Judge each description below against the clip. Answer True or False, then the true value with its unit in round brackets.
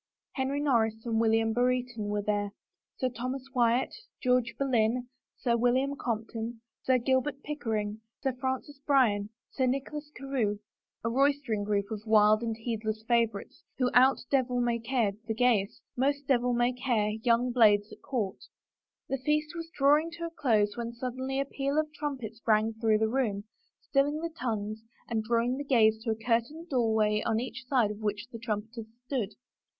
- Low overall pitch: False (240 Hz)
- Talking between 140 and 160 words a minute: False (175 wpm)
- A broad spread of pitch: False (3.4 semitones)